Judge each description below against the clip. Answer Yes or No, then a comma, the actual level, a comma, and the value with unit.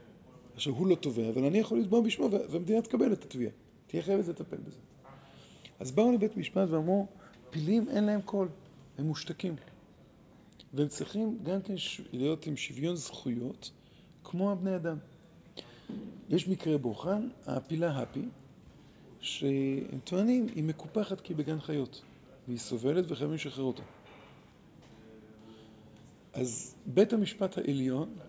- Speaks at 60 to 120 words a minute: No, average, 130 wpm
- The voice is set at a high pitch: No, medium, 165 Hz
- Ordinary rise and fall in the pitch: No, wide, 6.3 semitones